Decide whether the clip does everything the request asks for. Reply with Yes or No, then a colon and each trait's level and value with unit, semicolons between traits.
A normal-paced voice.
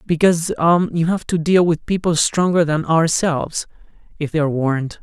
Yes: average, 165 wpm